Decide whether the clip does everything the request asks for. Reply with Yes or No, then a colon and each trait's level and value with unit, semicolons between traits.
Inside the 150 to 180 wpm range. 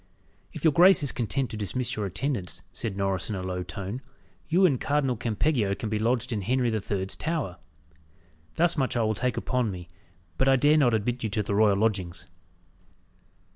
No: average, 195 wpm